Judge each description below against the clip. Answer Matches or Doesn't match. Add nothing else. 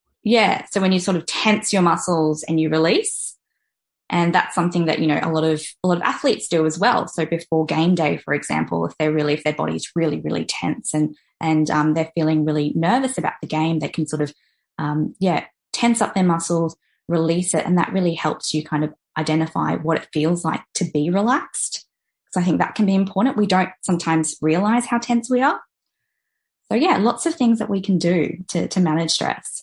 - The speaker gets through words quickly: Matches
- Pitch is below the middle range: Doesn't match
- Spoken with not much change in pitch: Doesn't match